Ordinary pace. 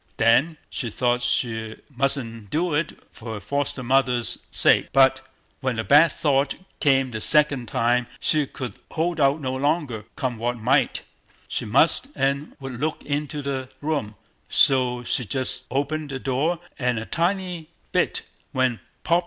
Yes: average, 150 wpm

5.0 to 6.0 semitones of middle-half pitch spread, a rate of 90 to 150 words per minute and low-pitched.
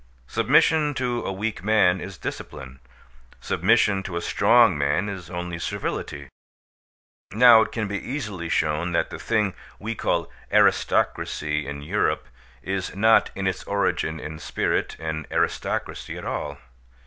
Yes: wide, 5.5 semitones; average, 140 wpm; very low, 95 Hz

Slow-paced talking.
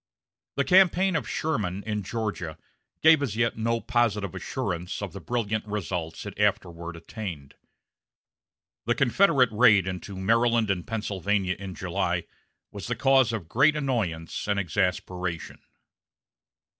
Yes: slow, 130 wpm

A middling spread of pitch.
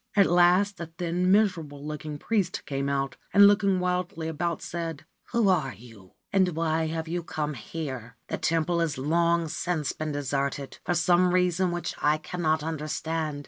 Yes: average, 3.1 semitones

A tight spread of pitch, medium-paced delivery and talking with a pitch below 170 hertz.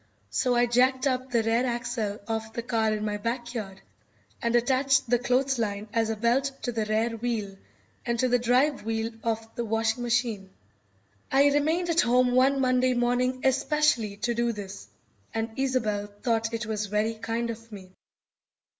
No: narrow, 2.3 semitones; average, 170 wpm; high, 235 Hz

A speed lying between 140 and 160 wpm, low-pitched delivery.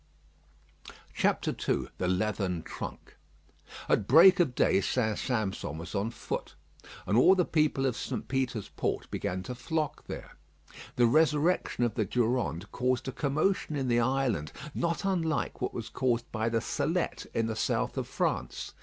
Yes: average, 155 wpm; low, 125 Hz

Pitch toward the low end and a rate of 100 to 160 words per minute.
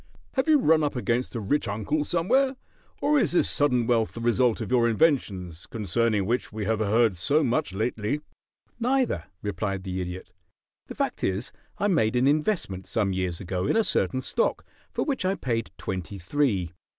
No: low, 115 Hz; average, 180 wpm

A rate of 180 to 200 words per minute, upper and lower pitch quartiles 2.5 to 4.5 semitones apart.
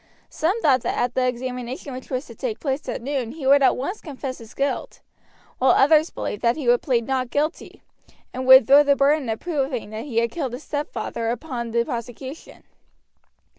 Yes: average, 195 wpm; average, 3.0 semitones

